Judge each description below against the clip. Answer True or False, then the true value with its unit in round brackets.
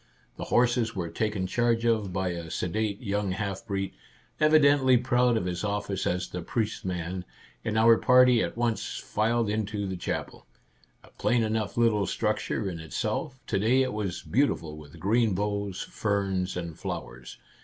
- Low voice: True (105 Hz)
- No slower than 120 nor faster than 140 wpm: False (165 wpm)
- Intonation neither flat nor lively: True (3.8 semitones)